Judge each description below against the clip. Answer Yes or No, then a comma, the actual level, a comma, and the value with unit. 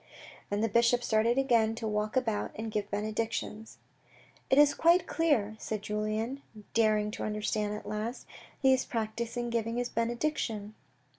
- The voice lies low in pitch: No, high, 225 Hz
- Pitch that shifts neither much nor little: No, narrow, 2.2 semitones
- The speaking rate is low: No, average, 160 wpm